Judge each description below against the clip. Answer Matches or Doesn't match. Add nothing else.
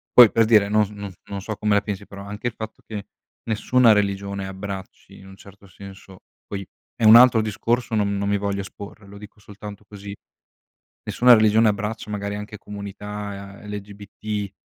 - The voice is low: Matches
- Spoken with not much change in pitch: Matches